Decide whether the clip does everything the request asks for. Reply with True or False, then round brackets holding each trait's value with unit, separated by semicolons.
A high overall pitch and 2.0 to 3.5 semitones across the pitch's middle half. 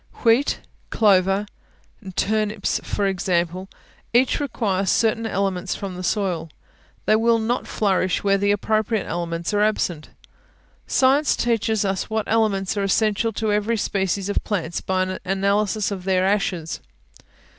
True (200 Hz; 2.7 semitones)